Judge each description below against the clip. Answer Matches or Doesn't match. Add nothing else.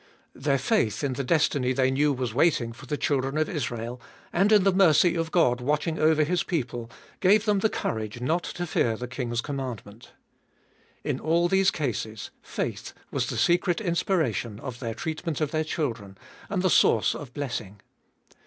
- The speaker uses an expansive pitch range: Matches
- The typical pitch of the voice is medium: Matches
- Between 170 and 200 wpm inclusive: Matches